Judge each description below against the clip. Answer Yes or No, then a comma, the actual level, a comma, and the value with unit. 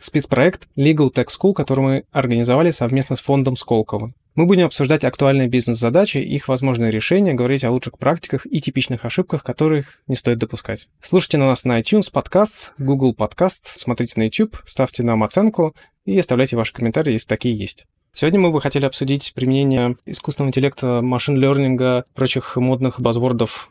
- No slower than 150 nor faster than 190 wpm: Yes, fast, 160 wpm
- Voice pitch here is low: Yes, low, 130 Hz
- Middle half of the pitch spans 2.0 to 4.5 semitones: Yes, average, 3.7 semitones